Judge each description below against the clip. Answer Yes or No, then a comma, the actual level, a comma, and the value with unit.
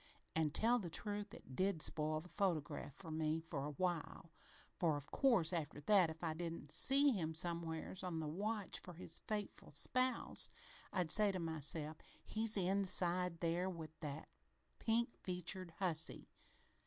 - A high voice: No, medium, 170 Hz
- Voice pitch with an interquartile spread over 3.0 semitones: Yes, average, 3.8 semitones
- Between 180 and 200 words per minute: No, average, 155 wpm